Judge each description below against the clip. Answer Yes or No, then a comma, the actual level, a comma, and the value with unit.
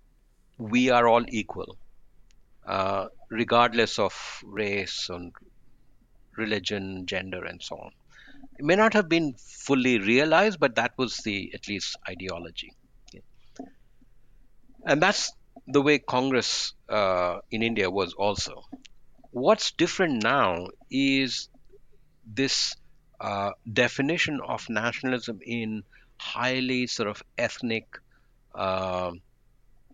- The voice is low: Yes, low, 115 Hz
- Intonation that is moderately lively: Yes, average, 3.9 semitones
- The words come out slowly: Yes, slow, 110 wpm